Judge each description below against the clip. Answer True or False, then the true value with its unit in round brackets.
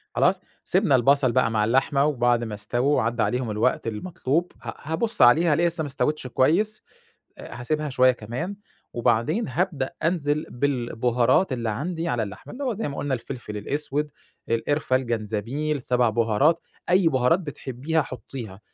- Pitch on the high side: False (130 Hz)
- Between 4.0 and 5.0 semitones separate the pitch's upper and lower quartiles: True (4.5 semitones)